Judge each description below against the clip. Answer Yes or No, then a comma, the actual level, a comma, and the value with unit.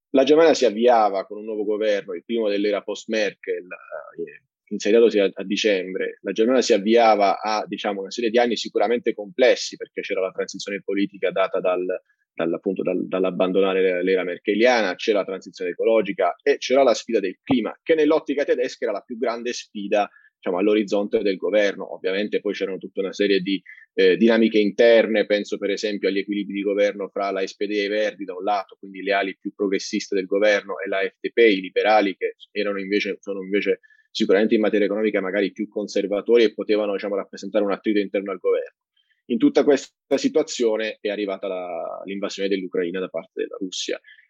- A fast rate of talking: Yes, fast, 175 wpm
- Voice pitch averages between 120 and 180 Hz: No, low, 105 Hz